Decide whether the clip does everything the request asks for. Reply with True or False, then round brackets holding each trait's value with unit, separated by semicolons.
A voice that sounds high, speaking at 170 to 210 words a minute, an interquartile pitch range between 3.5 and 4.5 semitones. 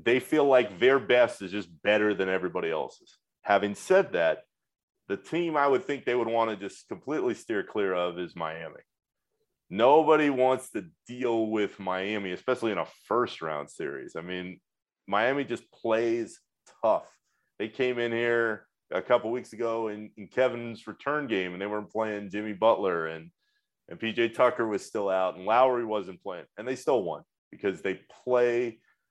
False (115 Hz; 175 wpm; 3.8 semitones)